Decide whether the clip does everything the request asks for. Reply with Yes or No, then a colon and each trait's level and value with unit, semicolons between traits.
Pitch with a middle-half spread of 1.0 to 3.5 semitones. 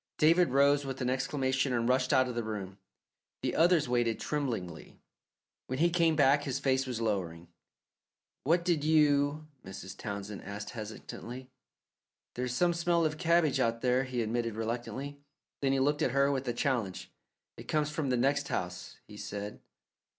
No: average, 4.1 semitones